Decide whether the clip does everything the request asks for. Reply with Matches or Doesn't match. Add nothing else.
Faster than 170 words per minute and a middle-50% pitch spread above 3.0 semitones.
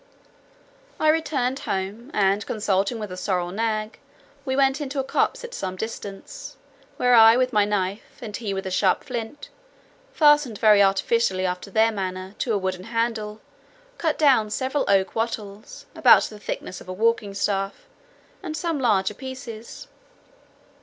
Doesn't match